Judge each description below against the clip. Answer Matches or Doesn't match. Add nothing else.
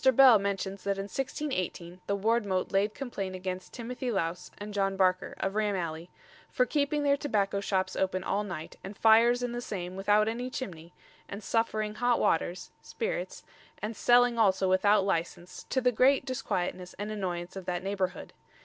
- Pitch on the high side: Matches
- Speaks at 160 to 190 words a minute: Matches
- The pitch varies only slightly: Doesn't match